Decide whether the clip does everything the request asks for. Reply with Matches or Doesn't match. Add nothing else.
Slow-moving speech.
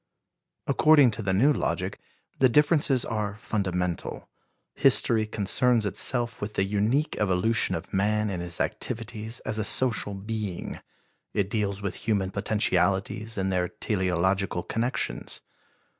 Matches